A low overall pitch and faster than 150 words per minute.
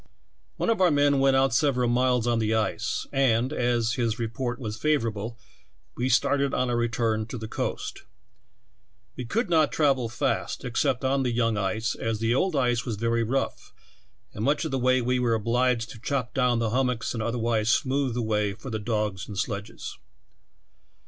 Yes: low, 120 Hz; average, 190 wpm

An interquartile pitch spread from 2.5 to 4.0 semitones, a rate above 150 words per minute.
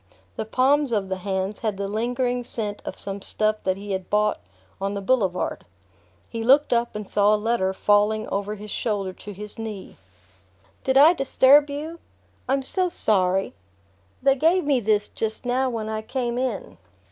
No: average, 4.4 semitones; average, 170 wpm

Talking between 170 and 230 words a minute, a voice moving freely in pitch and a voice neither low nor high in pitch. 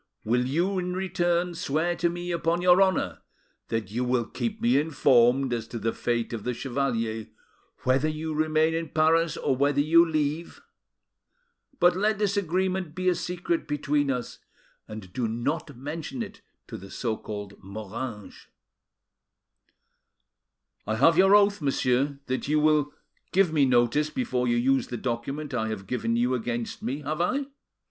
No: average, 160 wpm; wide, 6.1 semitones; medium, 145 Hz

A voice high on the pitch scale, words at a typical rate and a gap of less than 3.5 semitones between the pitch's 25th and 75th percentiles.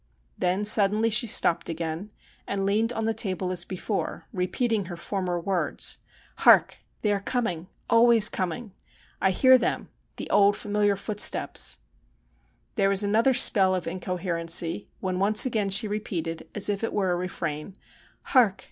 Yes: high, 195 Hz; average, 160 wpm; average, 2.9 semitones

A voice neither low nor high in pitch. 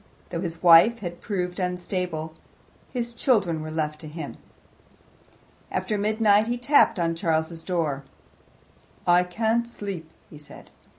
Yes: medium, 180 Hz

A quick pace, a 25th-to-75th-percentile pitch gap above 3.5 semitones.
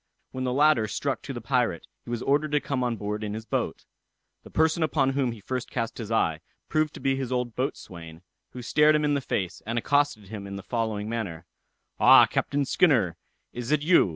Yes: fast, 215 wpm; average, 5.0 semitones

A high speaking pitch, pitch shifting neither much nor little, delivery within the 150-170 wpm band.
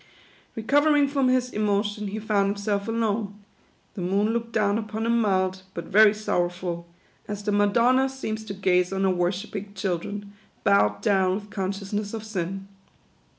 No: high, 205 Hz; narrow, 2.3 semitones; average, 155 wpm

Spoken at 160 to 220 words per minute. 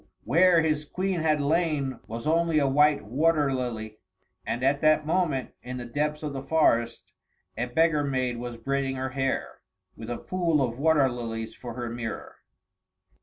Yes: average, 170 wpm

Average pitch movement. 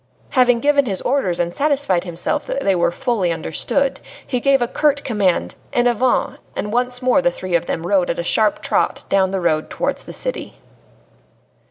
No: wide, 6.9 semitones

